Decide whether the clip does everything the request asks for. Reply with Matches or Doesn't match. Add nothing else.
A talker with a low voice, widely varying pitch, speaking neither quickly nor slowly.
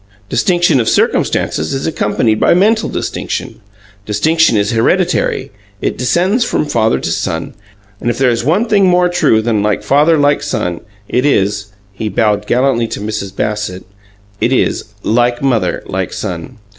Matches